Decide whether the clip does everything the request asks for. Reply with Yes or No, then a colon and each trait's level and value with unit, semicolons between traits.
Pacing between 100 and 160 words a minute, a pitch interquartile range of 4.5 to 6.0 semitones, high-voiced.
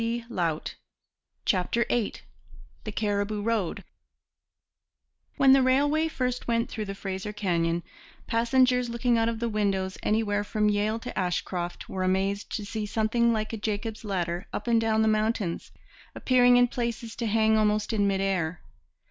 No: average, 150 wpm; average, 2.9 semitones; high, 215 Hz